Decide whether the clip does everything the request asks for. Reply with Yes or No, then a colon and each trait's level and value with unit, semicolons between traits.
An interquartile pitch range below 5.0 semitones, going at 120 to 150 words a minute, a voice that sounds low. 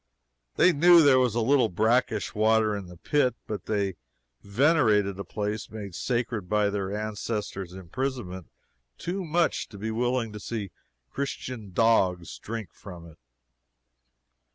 Yes: average, 4.1 semitones; average, 140 wpm; low, 110 Hz